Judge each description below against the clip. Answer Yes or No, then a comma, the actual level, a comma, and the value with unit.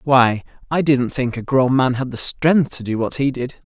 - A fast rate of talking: Yes, fast, 240 wpm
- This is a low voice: Yes, low, 130 Hz